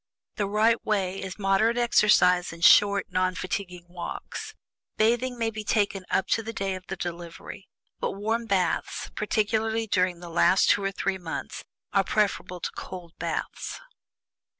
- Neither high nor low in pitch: No, high, 195 Hz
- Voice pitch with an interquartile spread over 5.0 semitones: No, average, 3.2 semitones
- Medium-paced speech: Yes, average, 155 wpm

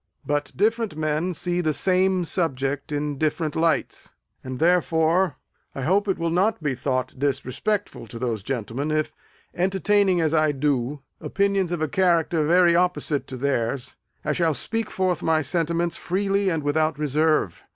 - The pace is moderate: Yes, average, 160 wpm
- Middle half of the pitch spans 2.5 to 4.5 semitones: Yes, average, 3.9 semitones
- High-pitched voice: No, medium, 160 Hz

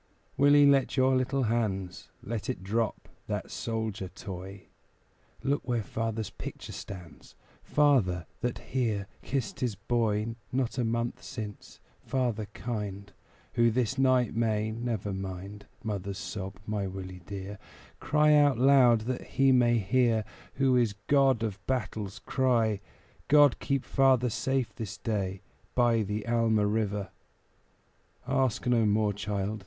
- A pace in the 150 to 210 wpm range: No, slow, 135 wpm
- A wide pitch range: No, average, 3.9 semitones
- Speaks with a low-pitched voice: Yes, low, 115 Hz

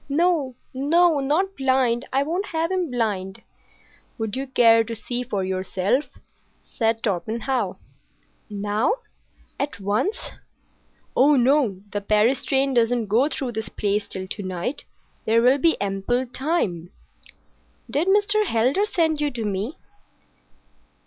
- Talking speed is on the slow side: Yes, slow, 130 wpm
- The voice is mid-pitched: No, high, 245 Hz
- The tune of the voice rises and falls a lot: Yes, wide, 5.8 semitones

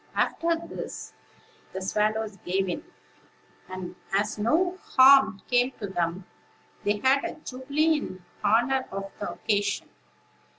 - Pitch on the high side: Yes, high, 215 Hz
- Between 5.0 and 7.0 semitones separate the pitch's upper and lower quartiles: Yes, wide, 5.5 semitones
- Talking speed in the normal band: No, slow, 125 wpm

